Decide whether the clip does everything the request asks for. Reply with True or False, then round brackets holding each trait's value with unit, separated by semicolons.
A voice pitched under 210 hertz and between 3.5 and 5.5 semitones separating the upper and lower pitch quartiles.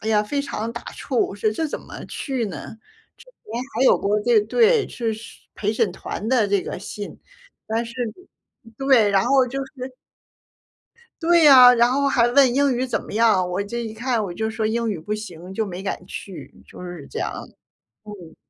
False (225 Hz; 4.0 semitones)